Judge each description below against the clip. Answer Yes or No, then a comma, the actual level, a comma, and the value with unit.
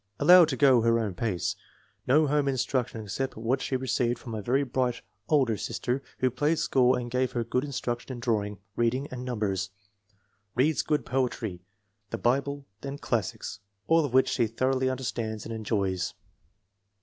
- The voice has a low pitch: Yes, low, 125 Hz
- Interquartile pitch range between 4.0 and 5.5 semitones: No, average, 2.9 semitones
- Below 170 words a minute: No, average, 175 wpm